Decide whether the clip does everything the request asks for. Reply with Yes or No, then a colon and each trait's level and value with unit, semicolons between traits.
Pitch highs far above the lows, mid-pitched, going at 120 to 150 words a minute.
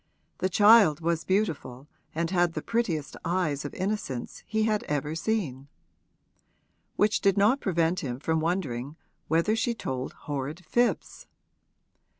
Yes: wide, 5.8 semitones; medium, 170 Hz; slow, 135 wpm